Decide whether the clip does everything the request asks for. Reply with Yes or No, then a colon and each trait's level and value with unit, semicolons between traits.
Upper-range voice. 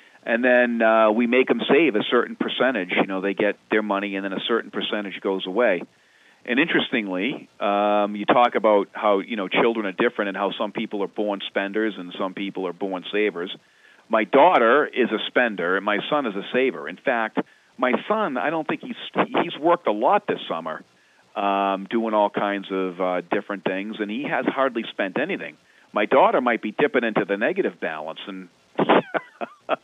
No: low, 100 Hz